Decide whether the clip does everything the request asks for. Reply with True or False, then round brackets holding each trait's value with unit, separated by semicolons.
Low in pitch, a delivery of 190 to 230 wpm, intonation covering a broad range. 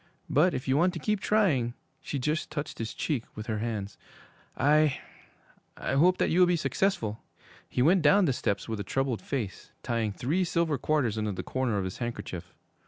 True (130 Hz; 195 wpm; 6.8 semitones)